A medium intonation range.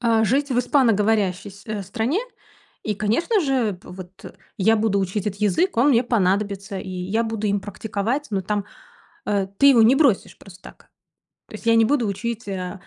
Yes: average, 3.0 semitones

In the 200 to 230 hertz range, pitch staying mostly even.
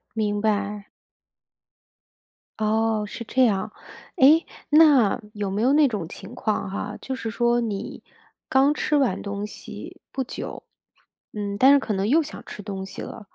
No: high, 220 Hz; average, 4.3 semitones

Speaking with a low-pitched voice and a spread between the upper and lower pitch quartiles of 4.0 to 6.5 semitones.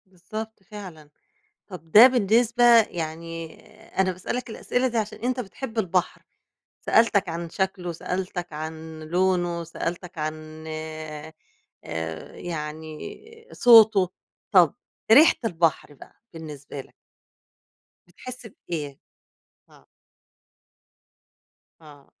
No: medium, 175 Hz; average, 5.3 semitones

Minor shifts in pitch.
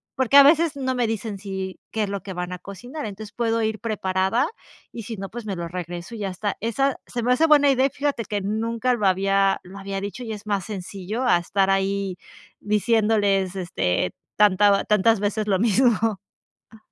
No: average, 3.1 semitones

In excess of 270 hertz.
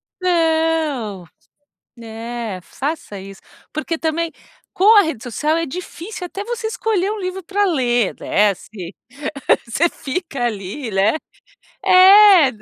Yes: very high, 315 Hz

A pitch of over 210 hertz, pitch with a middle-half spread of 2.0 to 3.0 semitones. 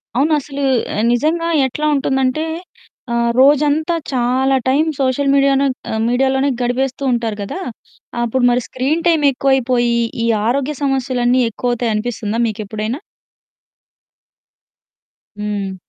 Yes: very high, 260 Hz; average, 2.7 semitones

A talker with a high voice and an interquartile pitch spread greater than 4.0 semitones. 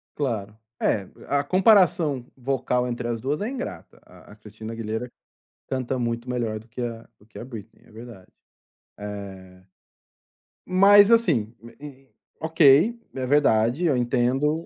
No: low, 125 Hz; average, 4.9 semitones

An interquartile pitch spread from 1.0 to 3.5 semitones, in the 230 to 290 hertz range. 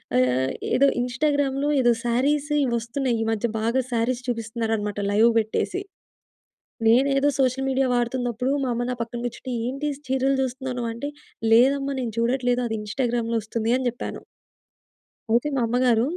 Yes: narrow, 2.4 semitones; high, 245 Hz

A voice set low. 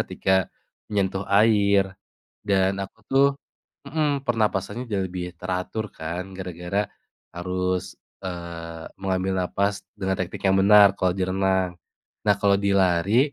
Yes: very low, 95 Hz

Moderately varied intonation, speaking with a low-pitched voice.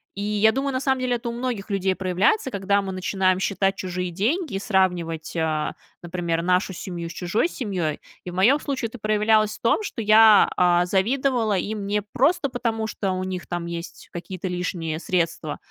No: average, 3.9 semitones; high, 195 Hz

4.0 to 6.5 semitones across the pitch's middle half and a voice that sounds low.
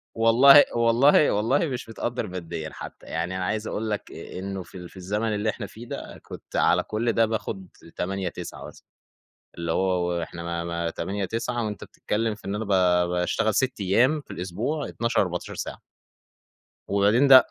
Yes: average, 4.3 semitones; low, 105 Hz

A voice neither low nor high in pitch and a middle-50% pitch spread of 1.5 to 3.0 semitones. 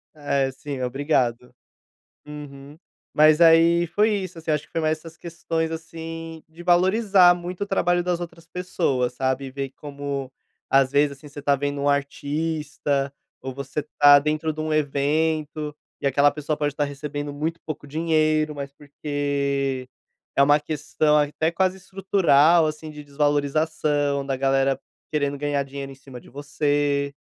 Yes: medium, 150 Hz; narrow, 2.5 semitones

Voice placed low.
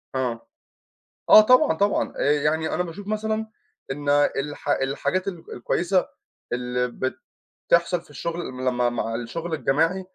No: medium, 155 Hz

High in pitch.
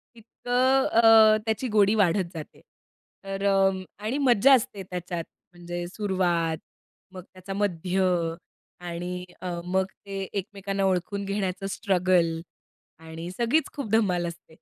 Yes: high, 195 Hz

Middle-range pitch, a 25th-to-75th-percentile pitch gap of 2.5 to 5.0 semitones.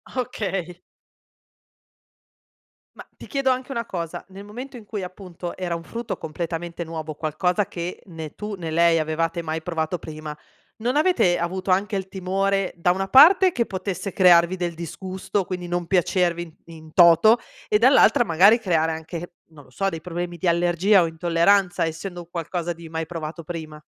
Yes: medium, 175 Hz; average, 2.9 semitones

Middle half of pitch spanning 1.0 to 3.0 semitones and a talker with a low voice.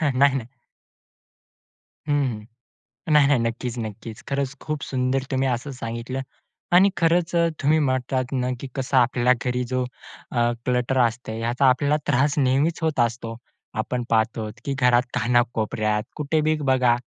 Yes: average, 2.7 semitones; low, 130 Hz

